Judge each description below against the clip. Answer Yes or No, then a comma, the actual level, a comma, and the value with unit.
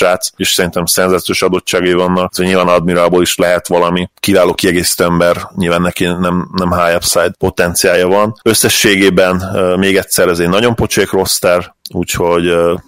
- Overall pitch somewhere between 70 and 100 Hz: Yes, very low, 90 Hz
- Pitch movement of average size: No, narrow, 1.0 semitones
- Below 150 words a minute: No, fast, 155 wpm